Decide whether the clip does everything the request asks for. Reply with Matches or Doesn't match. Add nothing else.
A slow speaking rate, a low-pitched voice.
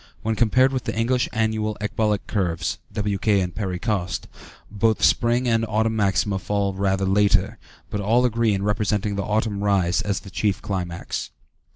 Doesn't match